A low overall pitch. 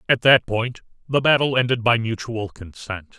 Yes: low, 115 Hz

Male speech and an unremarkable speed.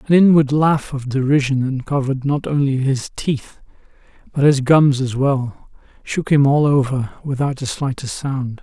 Yes: male; average, 160 wpm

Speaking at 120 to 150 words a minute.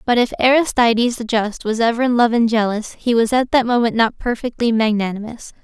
No: average, 200 wpm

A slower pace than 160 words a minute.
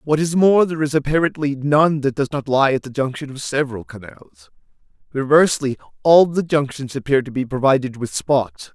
No: average, 185 wpm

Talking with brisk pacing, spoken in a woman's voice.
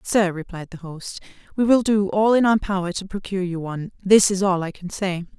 Yes: fast, 225 wpm; female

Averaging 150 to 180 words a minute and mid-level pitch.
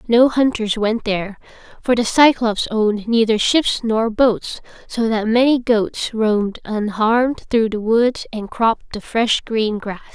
No: average, 160 wpm; high, 225 Hz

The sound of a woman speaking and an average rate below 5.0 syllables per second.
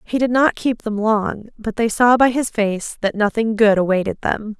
Yes: female; 4.7 syllables/s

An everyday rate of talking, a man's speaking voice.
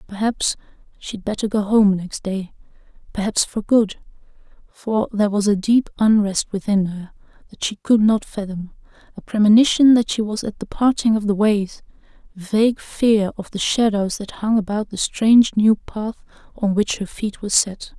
No: average, 170 wpm; female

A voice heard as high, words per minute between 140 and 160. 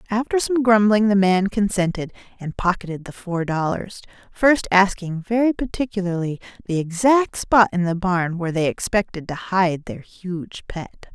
Yes: high, 195 Hz; average, 155 wpm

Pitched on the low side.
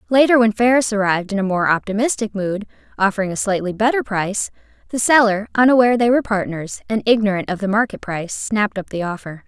No: high, 210 Hz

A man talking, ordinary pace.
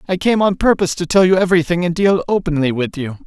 No: male; fast, 240 wpm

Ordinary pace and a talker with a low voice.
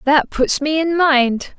No: average, 190 wpm; very high, 290 Hz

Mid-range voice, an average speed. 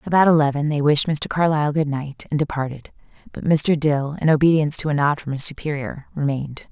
Yes: medium, 150 Hz; average, 195 wpm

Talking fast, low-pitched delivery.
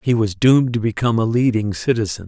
Yes: fast, 210 wpm; low, 115 Hz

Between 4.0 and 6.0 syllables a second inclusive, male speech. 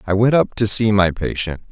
Yes: 5.3 syllables/s; male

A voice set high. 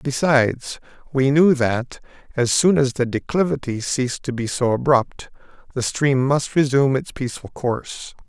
No: low, 135 Hz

